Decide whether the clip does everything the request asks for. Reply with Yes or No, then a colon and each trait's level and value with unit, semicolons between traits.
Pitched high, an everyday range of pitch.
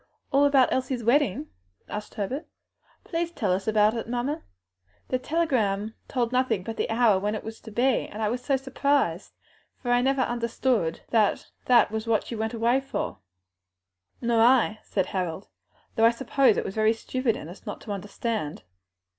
Yes: high, 230 Hz; average, 3.4 semitones